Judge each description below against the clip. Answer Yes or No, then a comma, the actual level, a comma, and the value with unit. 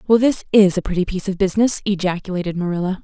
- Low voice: No, high, 190 Hz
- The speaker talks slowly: No, average, 200 wpm